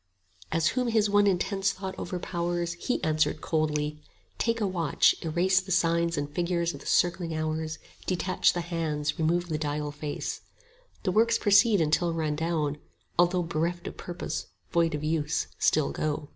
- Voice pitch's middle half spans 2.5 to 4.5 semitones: Yes, average, 2.9 semitones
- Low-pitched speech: No, medium, 170 Hz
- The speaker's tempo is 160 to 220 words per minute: Yes, average, 170 wpm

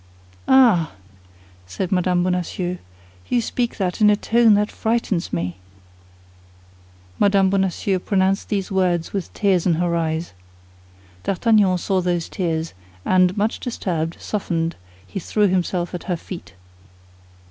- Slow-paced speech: Yes, slow, 125 wpm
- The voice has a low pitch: No, medium, 185 Hz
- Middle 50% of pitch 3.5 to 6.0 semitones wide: No, average, 2.8 semitones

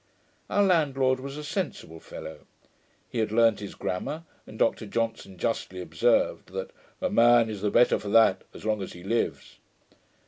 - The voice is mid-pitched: No, low, 115 Hz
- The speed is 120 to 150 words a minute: No, average, 175 wpm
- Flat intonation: No, average, 4.6 semitones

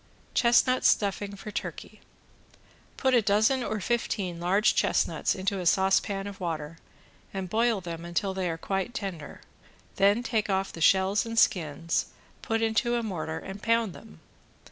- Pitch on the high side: Yes, high, 195 Hz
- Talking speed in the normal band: Yes, average, 155 wpm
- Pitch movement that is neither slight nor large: Yes, average, 3.9 semitones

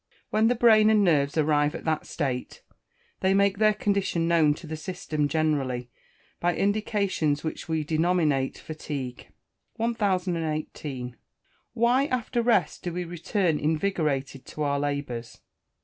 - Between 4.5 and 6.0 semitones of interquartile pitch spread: Yes, average, 5.3 semitones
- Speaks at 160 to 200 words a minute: No, slow, 135 wpm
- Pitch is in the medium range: Yes, medium, 160 Hz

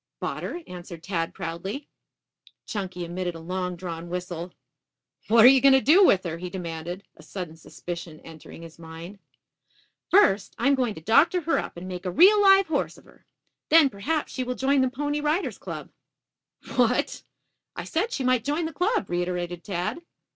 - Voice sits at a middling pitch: No, high, 195 Hz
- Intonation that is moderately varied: No, wide, 8.5 semitones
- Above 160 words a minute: Yes, average, 185 wpm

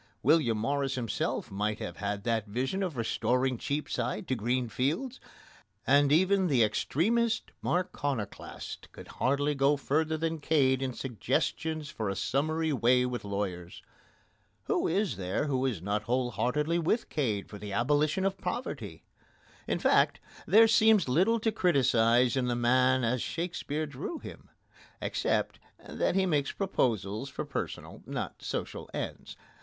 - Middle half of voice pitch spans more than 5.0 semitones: Yes, wide, 5.4 semitones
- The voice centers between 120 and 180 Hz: Yes, low, 135 Hz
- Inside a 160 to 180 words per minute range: No, average, 150 wpm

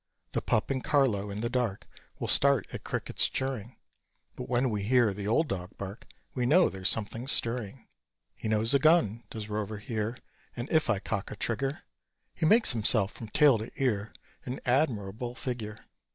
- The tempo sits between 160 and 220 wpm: Yes, average, 180 wpm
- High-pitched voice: No, low, 115 Hz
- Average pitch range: Yes, average, 3.7 semitones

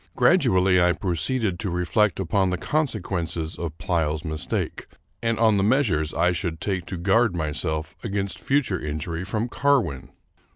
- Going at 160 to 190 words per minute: No, average, 150 wpm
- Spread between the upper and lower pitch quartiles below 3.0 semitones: No, average, 4.4 semitones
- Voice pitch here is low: Yes, very low, 90 Hz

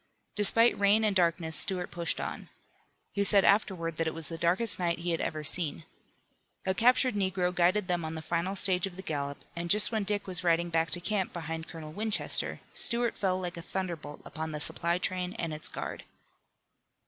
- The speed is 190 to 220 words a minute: Yes, average, 195 wpm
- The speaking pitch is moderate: Yes, medium, 180 Hz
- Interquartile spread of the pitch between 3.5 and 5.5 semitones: No, average, 3.1 semitones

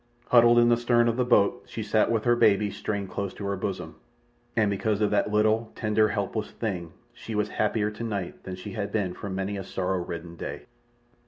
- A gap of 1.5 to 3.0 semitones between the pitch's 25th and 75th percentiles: Yes, narrow, 2.4 semitones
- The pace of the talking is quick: Yes, fast, 210 wpm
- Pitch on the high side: No, low, 105 Hz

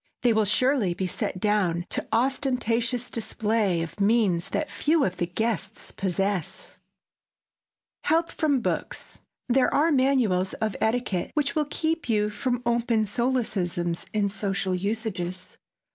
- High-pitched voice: Yes, high, 220 Hz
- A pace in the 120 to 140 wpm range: Yes, slow, 135 wpm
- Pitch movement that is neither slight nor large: Yes, average, 4.9 semitones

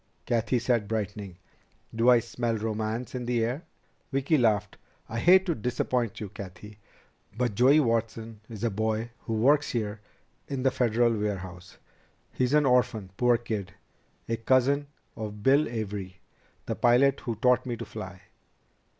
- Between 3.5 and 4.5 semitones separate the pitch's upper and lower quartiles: No, average, 3.0 semitones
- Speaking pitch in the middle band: No, low, 115 Hz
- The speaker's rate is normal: Yes, average, 150 wpm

